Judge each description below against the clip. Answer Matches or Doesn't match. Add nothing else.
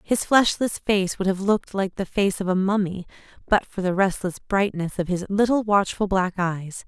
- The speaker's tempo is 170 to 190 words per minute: Doesn't match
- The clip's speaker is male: Doesn't match